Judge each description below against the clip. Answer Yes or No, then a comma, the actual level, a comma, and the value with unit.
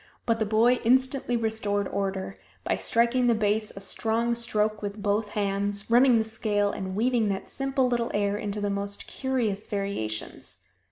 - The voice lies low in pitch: No, high, 215 Hz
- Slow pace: No, average, 165 wpm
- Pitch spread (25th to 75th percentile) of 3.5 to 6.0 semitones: No, narrow, 2.6 semitones